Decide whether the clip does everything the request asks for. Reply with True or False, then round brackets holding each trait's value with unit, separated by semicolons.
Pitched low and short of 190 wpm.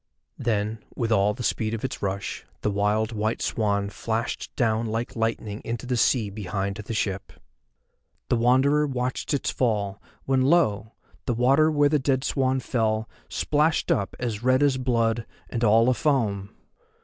True (115 Hz; 160 wpm)